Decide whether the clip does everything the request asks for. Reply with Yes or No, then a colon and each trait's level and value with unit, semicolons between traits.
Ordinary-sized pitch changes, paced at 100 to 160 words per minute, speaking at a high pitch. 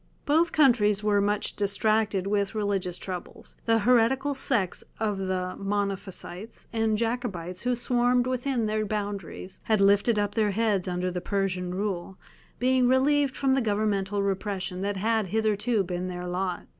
Yes: average, 3.2 semitones; average, 150 wpm; high, 205 Hz